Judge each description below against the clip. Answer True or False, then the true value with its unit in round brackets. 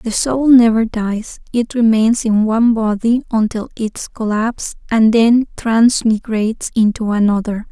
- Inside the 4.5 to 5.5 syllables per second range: False (4.2 syllables/s)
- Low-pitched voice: False (225 Hz)